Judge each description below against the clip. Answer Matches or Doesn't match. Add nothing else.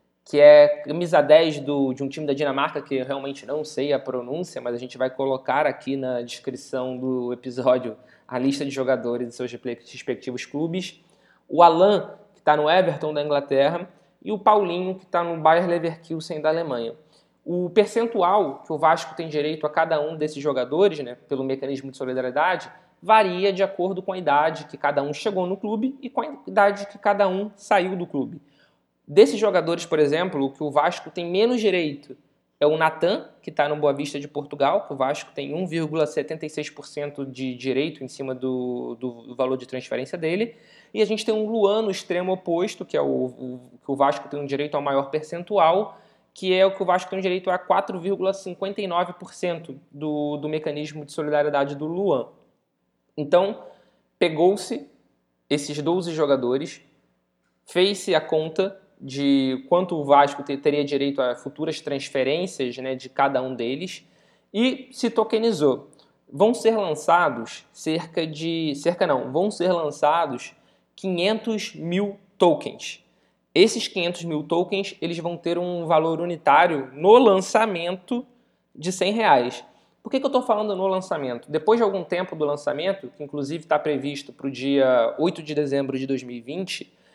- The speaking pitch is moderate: Matches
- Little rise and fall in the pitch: Doesn't match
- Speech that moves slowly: Doesn't match